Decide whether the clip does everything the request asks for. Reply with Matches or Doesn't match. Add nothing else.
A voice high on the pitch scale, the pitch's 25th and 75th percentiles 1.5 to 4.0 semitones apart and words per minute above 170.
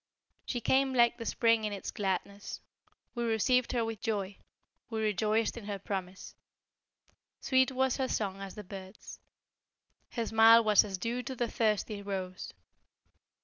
Doesn't match